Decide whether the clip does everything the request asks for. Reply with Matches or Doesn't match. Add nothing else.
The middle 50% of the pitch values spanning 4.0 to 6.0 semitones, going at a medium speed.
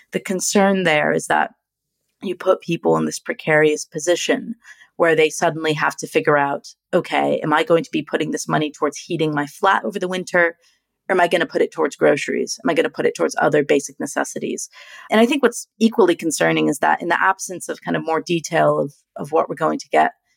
Doesn't match